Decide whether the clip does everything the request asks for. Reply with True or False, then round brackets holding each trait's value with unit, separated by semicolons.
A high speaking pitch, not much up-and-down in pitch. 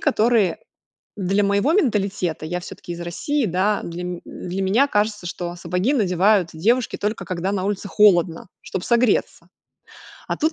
False (195 Hz; 3.4 semitones)